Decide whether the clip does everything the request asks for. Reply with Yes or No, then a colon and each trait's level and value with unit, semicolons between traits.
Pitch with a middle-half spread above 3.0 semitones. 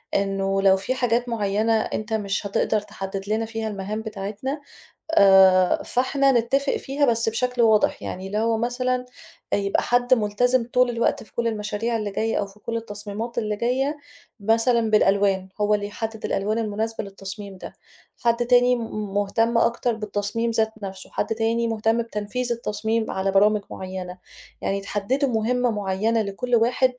No: average, 2.7 semitones